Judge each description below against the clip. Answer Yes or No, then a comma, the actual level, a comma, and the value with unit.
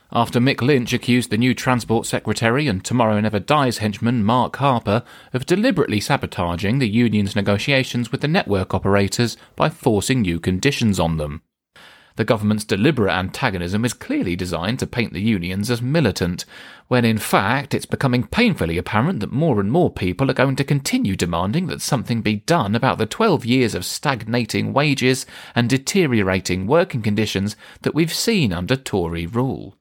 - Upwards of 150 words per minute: Yes, average, 165 wpm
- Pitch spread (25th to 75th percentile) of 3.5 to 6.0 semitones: Yes, average, 4.6 semitones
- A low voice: Yes, low, 115 Hz